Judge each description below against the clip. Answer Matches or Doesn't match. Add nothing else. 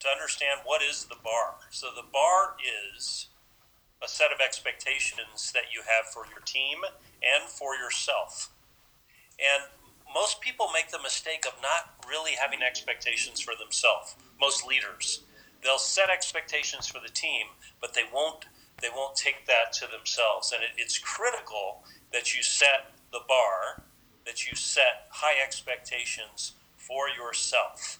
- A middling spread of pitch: Matches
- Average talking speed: Matches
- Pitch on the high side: Doesn't match